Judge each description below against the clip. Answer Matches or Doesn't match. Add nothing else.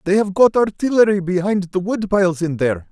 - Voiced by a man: Matches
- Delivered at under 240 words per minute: Matches